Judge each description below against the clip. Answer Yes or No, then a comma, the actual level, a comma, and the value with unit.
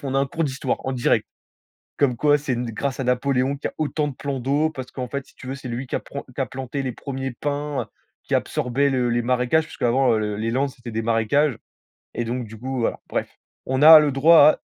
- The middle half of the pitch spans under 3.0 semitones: Yes, narrow, 2.5 semitones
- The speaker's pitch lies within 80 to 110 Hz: No, low, 130 Hz